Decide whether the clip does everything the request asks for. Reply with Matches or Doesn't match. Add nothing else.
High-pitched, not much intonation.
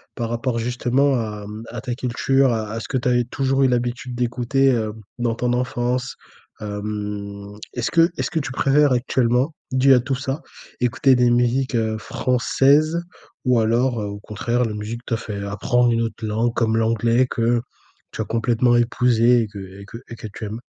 Doesn't match